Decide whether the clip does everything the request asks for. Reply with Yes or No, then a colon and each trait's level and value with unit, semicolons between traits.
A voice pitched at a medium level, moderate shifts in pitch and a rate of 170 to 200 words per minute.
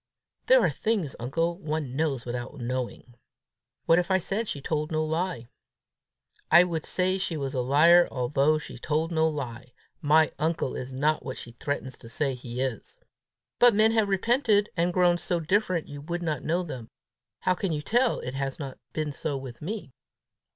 Yes: medium, 155 Hz; average, 5.0 semitones; average, 185 wpm